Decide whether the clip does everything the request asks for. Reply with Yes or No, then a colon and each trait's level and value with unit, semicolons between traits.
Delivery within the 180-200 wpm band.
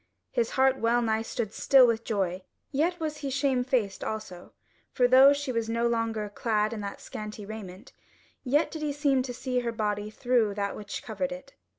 Yes: average, 195 wpm